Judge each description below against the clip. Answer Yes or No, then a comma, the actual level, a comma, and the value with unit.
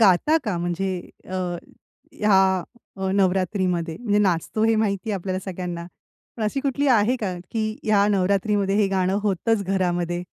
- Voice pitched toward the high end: Yes, high, 195 Hz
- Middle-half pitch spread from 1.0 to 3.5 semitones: Yes, average, 2.8 semitones